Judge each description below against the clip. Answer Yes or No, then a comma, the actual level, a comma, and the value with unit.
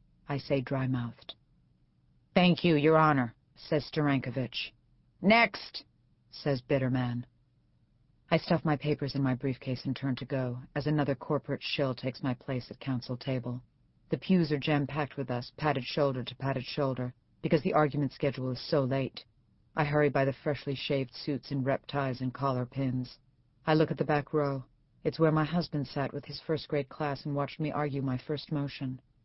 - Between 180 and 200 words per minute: Yes, average, 185 wpm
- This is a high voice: No, medium, 140 Hz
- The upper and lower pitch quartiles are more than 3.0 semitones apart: No, narrow, 2.5 semitones